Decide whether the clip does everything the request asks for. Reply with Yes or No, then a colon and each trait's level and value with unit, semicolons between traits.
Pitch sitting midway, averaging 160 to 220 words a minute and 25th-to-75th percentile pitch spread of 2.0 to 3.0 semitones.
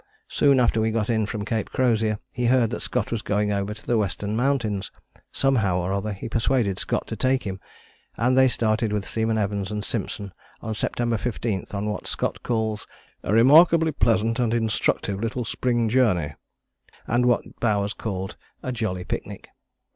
No: low, 110 Hz; average, 175 wpm; average, 2.7 semitones